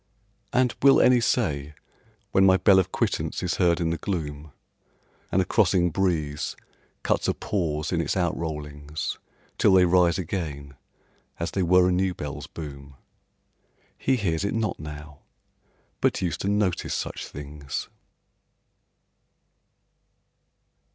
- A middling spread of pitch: Yes, average, 4.1 semitones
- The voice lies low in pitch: Yes, very low, 85 Hz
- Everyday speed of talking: No, slow, 130 wpm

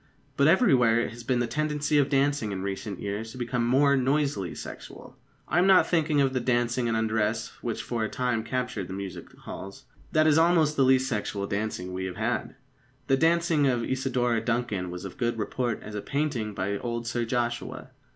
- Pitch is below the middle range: Yes, low, 120 Hz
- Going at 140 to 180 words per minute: No, average, 200 wpm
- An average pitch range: Yes, average, 4.2 semitones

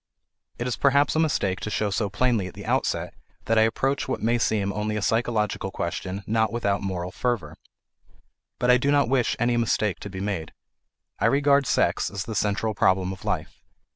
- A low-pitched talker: Yes, low, 110 Hz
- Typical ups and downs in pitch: Yes, average, 3.7 semitones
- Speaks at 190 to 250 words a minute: Yes, average, 195 wpm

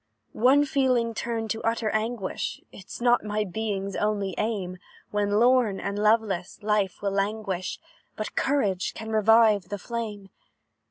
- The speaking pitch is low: No, high, 215 Hz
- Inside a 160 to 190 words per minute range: No, average, 140 wpm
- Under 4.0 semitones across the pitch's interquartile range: Yes, narrow, 2.4 semitones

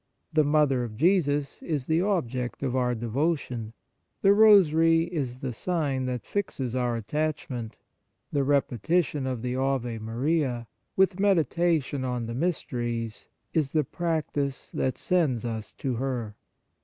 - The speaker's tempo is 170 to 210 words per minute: No, slow, 135 wpm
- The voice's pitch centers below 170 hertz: Yes, low, 135 Hz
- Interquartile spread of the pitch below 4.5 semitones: No, average, 4.8 semitones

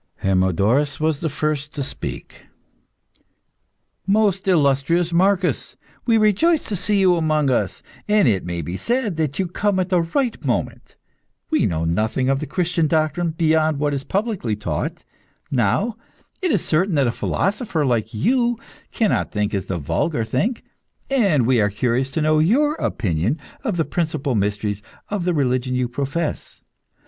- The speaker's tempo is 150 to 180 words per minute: Yes, average, 160 wpm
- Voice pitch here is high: No, medium, 155 Hz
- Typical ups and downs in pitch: No, wide, 7.7 semitones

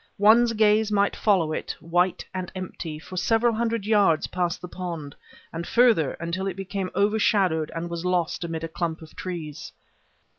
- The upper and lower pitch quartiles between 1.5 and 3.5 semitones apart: No, average, 3.9 semitones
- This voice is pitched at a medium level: Yes, medium, 180 Hz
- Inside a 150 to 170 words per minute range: Yes, average, 165 wpm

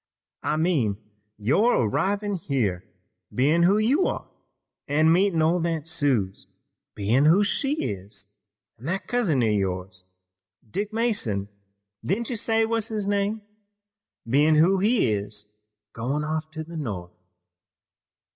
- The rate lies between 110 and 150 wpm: Yes, slow, 135 wpm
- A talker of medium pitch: Yes, medium, 155 Hz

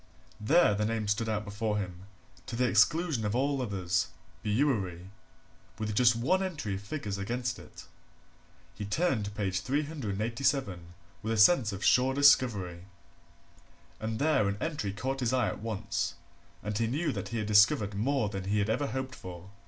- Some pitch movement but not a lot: Yes, average, 4.6 semitones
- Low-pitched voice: Yes, low, 110 Hz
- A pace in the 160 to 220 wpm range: Yes, average, 170 wpm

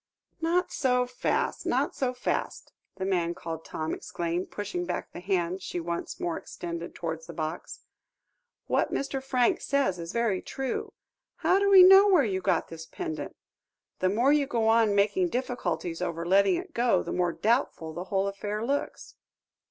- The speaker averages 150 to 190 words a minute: Yes, average, 170 wpm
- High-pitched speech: Yes, high, 200 Hz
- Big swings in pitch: Yes, wide, 7.2 semitones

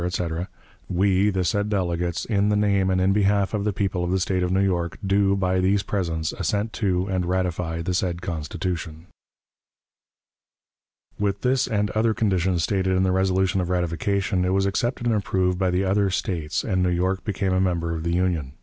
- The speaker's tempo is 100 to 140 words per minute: No, average, 195 wpm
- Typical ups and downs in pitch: No, narrow, 1.9 semitones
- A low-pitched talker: Yes, very low, 95 Hz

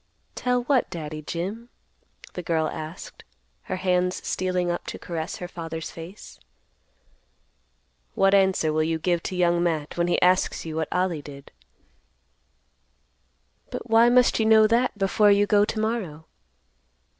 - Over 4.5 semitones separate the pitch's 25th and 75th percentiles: No, average, 4.1 semitones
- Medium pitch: Yes, medium, 180 Hz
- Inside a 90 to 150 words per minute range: Yes, average, 145 wpm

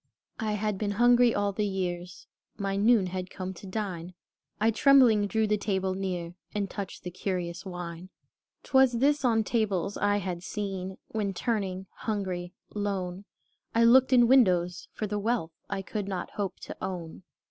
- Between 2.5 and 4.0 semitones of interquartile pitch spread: Yes, average, 2.9 semitones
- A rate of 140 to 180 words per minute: Yes, average, 170 wpm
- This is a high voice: Yes, high, 200 Hz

